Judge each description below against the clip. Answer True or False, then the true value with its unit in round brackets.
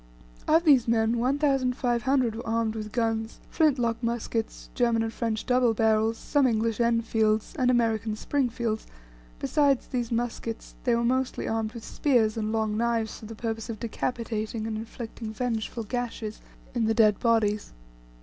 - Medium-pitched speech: False (230 Hz)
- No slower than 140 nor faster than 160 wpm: True (155 wpm)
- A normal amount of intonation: False (1.7 semitones)